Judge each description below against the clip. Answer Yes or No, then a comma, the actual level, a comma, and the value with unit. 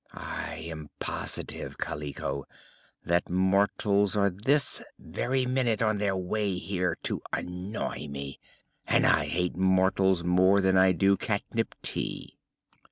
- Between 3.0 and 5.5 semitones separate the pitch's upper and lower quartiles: No, narrow, 2.4 semitones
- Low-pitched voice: Yes, very low, 95 Hz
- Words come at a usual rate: No, slow, 125 wpm